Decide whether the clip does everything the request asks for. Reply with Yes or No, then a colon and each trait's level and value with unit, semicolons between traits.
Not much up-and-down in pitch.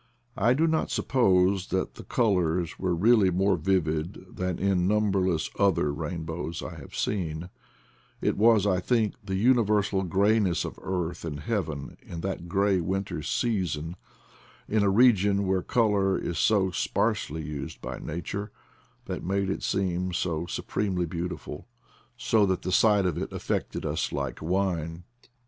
No: average, 3.0 semitones